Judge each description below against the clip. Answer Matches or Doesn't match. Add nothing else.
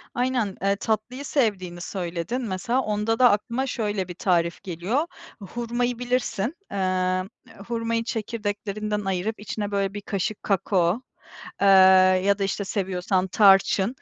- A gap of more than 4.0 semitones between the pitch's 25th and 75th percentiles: Doesn't match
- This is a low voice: Doesn't match